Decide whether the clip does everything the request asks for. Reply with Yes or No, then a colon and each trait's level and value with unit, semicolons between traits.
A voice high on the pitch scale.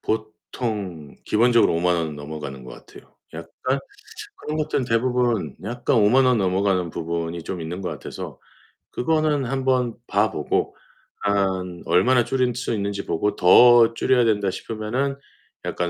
No: low, 105 Hz